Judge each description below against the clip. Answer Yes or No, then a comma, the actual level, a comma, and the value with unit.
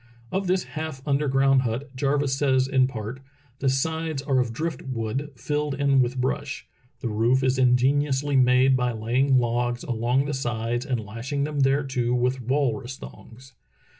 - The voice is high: No, low, 130 Hz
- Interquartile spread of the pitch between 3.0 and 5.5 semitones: No, narrow, 2.5 semitones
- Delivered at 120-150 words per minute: No, average, 160 wpm